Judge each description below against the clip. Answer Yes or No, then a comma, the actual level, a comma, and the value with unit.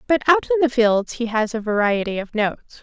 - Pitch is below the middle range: No, high, 230 Hz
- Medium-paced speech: No, fast, 235 wpm